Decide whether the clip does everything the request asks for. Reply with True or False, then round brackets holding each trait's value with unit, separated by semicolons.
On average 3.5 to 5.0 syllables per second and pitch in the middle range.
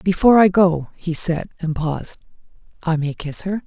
True (4.9 syllables/s; 170 Hz)